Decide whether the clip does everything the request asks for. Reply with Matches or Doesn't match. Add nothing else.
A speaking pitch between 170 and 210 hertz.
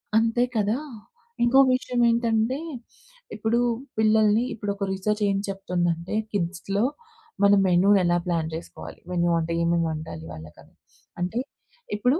Matches